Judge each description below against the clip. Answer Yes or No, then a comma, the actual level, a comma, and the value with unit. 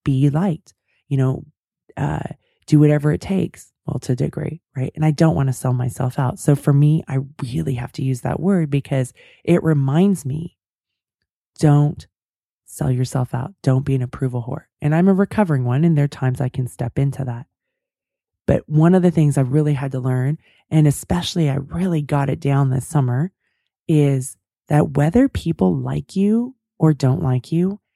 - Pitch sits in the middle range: Yes, medium, 145 Hz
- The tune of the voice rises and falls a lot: No, average, 3.6 semitones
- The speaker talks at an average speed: Yes, average, 185 wpm